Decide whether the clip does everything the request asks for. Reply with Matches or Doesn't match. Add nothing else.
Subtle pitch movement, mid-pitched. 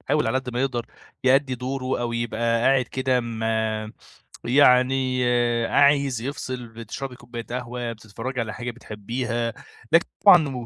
Doesn't match